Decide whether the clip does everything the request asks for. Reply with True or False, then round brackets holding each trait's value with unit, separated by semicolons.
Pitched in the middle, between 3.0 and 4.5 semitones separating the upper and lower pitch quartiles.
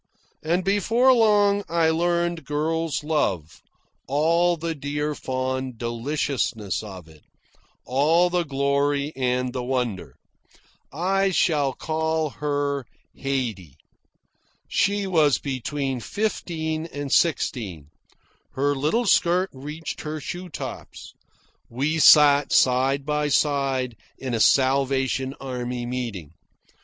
True (145 Hz; 4.1 semitones)